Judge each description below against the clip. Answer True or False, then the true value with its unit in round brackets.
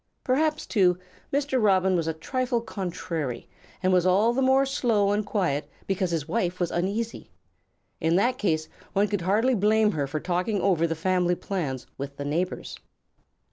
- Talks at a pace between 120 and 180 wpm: True (170 wpm)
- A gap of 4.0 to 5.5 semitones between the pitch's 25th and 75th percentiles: True (4.7 semitones)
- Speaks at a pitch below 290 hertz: True (190 Hz)